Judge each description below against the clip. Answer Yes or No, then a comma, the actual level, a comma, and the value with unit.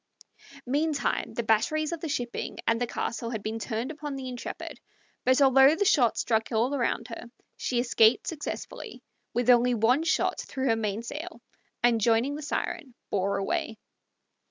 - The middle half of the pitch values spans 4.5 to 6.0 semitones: No, average, 4.0 semitones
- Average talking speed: Yes, average, 160 wpm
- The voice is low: No, high, 245 Hz